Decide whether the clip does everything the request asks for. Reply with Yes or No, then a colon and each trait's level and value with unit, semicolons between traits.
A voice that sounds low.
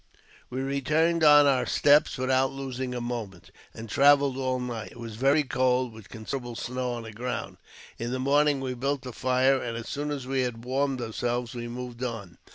Yes: low, 130 Hz